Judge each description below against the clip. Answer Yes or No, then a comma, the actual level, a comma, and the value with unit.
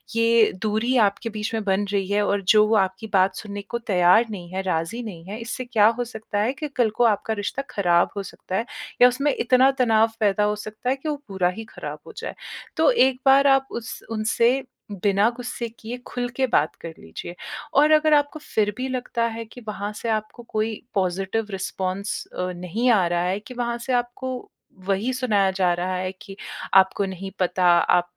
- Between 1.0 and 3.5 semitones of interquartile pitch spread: No, average, 4.1 semitones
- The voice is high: Yes, high, 215 Hz